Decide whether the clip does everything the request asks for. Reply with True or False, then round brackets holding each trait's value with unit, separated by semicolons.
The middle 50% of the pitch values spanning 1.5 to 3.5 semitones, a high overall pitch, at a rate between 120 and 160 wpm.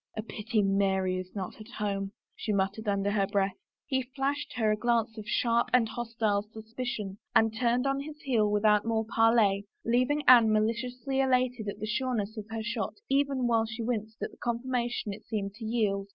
False (2.9 semitones; 225 Hz; 195 wpm)